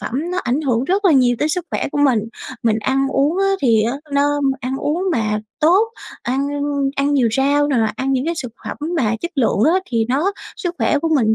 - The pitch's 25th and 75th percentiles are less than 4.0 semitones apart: No, average, 4.3 semitones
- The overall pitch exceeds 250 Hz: Yes, very high, 275 Hz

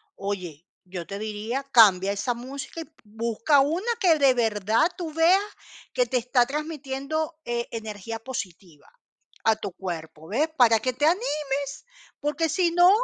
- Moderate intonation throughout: No, wide, 6.5 semitones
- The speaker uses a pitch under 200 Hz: No, high, 245 Hz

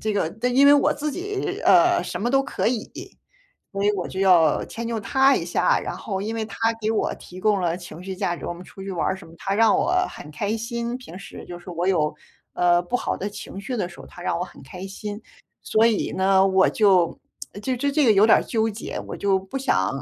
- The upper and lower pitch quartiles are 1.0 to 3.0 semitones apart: No, average, 4.2 semitones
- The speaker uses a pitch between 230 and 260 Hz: No, high, 200 Hz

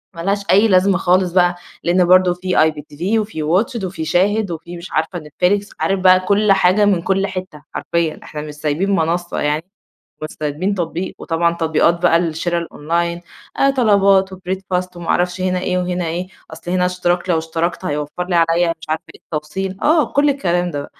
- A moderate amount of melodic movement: No, narrow, 2.3 semitones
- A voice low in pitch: No, medium, 180 Hz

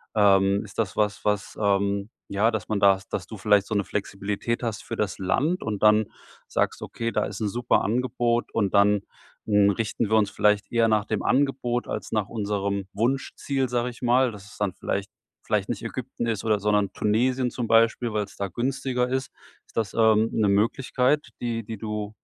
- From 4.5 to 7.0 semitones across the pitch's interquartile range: No, average, 2.7 semitones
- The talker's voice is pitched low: Yes, low, 110 Hz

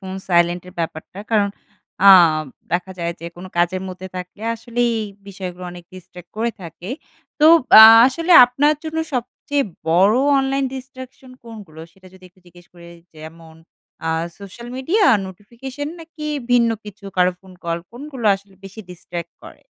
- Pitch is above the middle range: Yes, high, 195 Hz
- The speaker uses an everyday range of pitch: No, wide, 5.8 semitones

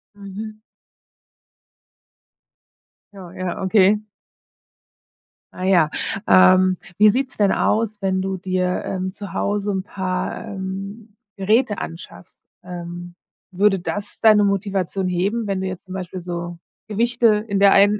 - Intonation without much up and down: Yes, narrow, 2.0 semitones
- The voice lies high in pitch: Yes, high, 195 Hz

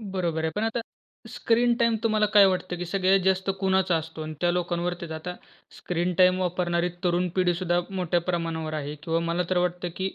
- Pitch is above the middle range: No, medium, 180 Hz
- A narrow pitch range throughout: Yes, narrow, 1.8 semitones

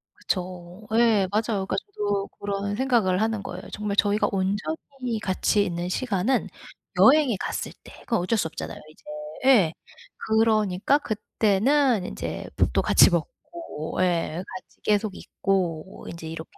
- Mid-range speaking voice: No, high, 205 Hz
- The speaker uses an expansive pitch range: No, average, 3.6 semitones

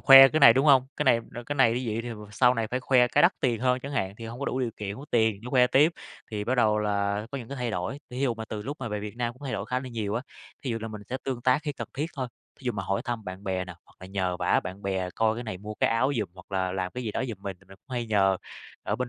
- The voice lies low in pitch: Yes, low, 115 Hz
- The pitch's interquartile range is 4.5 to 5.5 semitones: No, average, 4.0 semitones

